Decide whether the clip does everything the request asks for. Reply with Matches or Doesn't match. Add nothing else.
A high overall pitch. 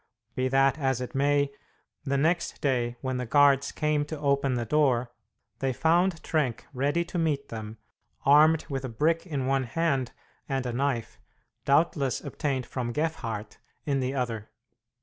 Doesn't match